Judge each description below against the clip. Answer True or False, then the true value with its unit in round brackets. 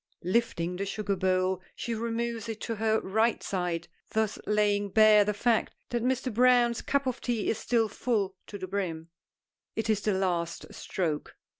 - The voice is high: True (210 Hz)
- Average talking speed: True (170 wpm)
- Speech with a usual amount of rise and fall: True (3.6 semitones)